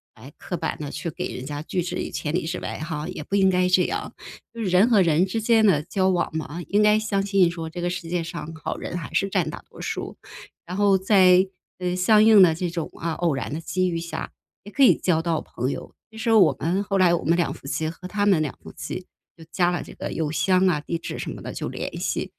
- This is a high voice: No, medium, 180 Hz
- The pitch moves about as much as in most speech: Yes, average, 3.0 semitones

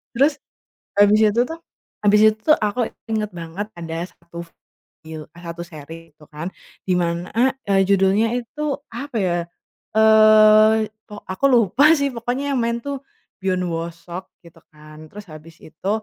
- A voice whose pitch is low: No, high, 205 Hz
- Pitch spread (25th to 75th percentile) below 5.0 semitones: No, wide, 5.5 semitones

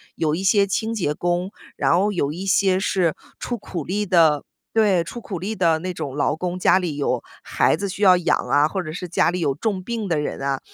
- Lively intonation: No, average, 3.5 semitones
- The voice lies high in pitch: No, medium, 180 Hz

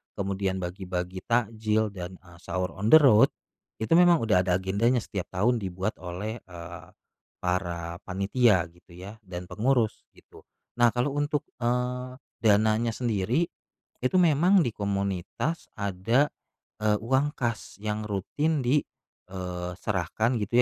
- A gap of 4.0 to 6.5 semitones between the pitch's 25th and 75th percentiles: Yes, average, 4.8 semitones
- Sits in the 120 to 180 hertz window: No, low, 105 Hz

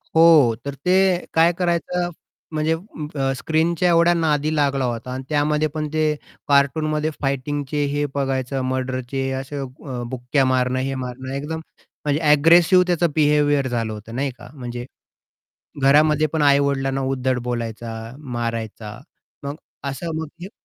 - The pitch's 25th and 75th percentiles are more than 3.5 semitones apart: No, average, 3.2 semitones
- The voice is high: No, medium, 140 Hz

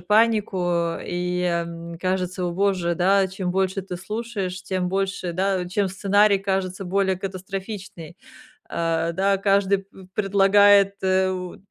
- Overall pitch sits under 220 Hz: Yes, high, 190 Hz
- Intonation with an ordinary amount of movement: No, narrow, 1.7 semitones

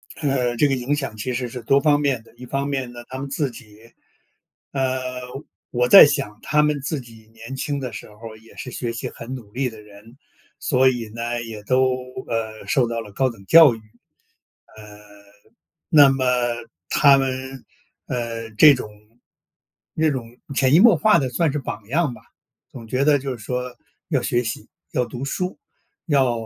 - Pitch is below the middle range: Yes, low, 125 Hz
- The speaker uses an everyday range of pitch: Yes, average, 3.2 semitones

